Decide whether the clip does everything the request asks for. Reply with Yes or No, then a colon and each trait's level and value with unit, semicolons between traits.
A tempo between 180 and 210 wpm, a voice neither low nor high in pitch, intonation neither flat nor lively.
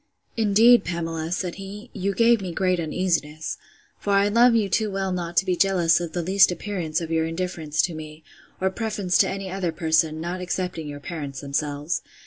Yes: average, 190 wpm; medium, 180 Hz; average, 3.4 semitones